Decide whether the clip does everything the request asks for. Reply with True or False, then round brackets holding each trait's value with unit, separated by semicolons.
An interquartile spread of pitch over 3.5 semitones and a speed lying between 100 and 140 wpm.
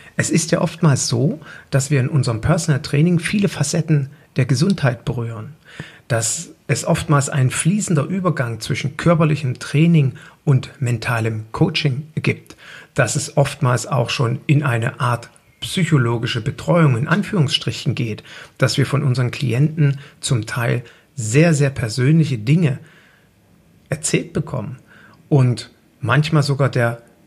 True (4.1 semitones; 130 wpm)